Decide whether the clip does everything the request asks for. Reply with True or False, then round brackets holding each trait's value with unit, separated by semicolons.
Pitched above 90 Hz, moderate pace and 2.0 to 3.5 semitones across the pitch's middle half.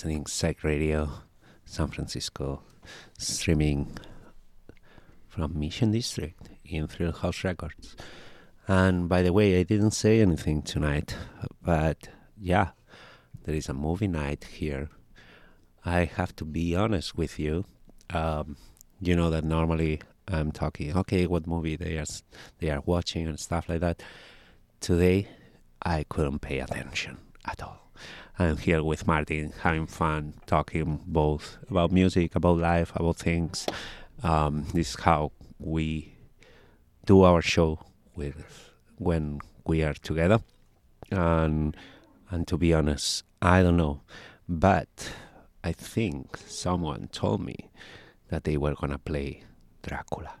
False (85 Hz; 130 wpm; 2.8 semitones)